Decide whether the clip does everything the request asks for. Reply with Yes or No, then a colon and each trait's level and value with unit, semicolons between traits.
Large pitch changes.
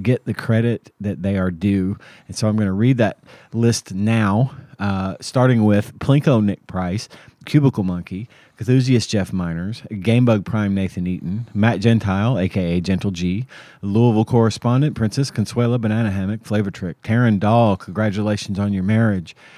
No: average, 3.3 semitones